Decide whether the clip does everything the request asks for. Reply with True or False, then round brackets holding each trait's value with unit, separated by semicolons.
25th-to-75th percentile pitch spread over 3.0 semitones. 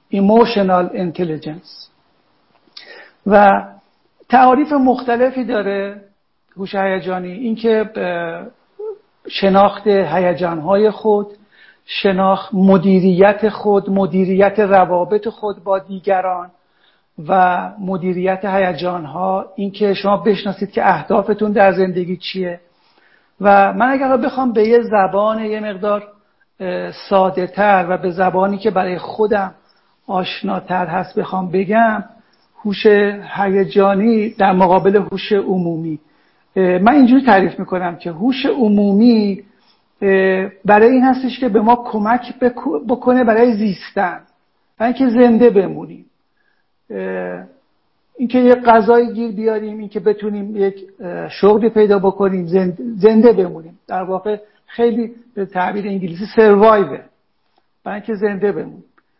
False (2.7 semitones)